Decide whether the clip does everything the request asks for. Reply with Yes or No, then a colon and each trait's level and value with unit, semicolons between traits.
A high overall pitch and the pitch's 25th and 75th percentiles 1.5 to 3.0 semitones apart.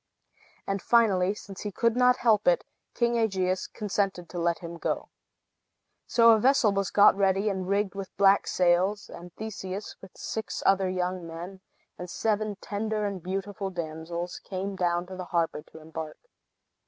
Yes: high, 195 Hz; average, 2.7 semitones